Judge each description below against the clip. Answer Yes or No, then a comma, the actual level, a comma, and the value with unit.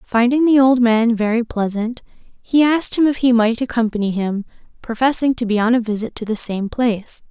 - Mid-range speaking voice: No, high, 235 Hz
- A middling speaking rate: Yes, average, 195 wpm